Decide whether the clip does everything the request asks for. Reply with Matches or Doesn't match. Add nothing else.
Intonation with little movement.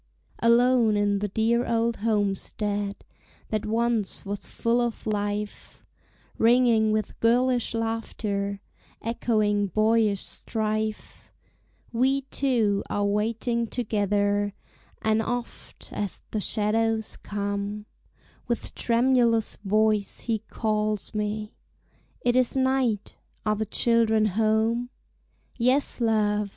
Matches